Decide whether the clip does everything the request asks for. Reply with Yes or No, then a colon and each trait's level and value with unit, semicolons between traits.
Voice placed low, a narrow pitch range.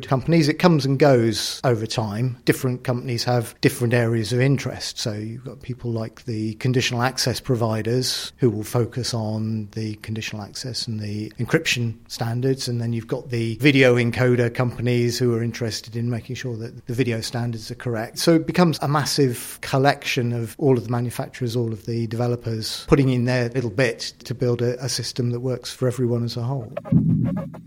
Yes: low, 120 Hz; narrow, 1.9 semitones